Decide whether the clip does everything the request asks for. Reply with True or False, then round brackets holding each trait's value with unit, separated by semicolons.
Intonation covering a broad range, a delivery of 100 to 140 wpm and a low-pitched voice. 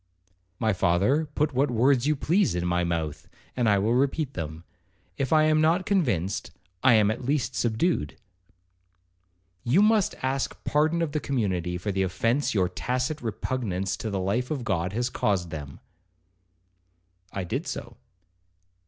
False (7.4 semitones; 155 wpm; 120 Hz)